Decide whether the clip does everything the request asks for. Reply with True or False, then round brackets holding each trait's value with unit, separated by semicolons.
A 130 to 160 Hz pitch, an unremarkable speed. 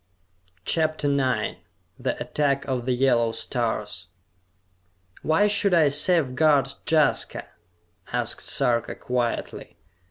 False (135 Hz; 95 wpm)